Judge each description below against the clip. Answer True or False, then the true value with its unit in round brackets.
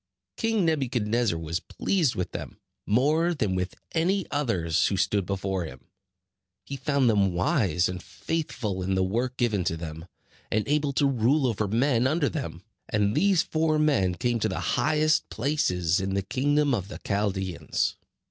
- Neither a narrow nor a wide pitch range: False (7.5 semitones)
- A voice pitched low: True (115 Hz)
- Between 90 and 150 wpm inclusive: False (165 wpm)